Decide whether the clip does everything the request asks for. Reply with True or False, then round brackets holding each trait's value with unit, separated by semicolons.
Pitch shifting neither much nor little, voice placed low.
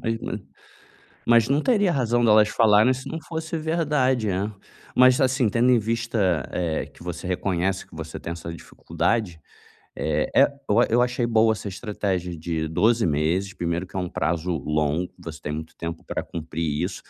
False (6.2 semitones; 100 Hz)